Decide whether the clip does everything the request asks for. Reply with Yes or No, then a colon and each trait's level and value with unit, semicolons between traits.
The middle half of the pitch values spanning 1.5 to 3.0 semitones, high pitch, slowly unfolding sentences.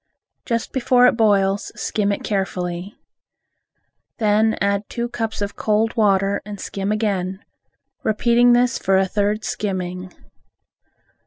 Yes: narrow, 2.4 semitones; high, 205 Hz; slow, 120 wpm